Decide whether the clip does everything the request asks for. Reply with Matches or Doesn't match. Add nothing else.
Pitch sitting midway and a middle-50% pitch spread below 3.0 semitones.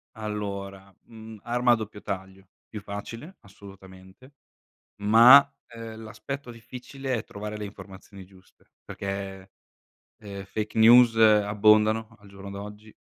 Doesn't match